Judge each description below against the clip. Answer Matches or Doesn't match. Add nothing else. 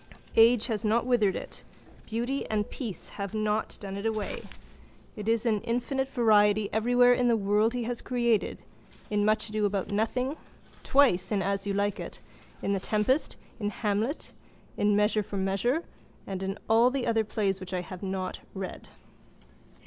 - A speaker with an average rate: Matches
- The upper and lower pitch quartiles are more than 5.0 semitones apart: Doesn't match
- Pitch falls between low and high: Doesn't match